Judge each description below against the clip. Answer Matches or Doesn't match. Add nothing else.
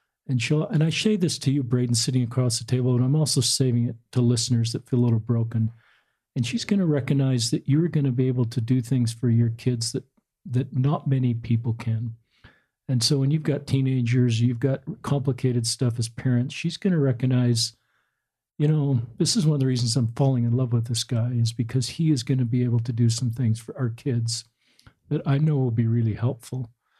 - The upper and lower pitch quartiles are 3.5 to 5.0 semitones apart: Doesn't match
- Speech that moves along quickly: Matches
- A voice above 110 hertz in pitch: Matches